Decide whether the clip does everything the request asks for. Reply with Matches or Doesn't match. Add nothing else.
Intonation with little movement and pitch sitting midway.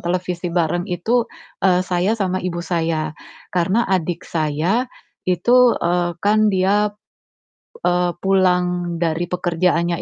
Matches